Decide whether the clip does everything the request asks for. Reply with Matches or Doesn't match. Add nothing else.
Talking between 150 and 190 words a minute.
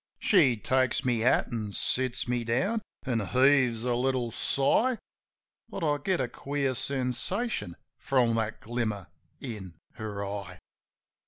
Doesn't match